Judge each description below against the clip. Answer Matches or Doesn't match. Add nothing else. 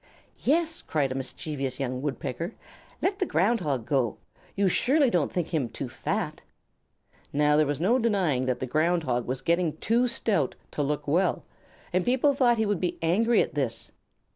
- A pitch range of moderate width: Doesn't match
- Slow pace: Doesn't match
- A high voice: Doesn't match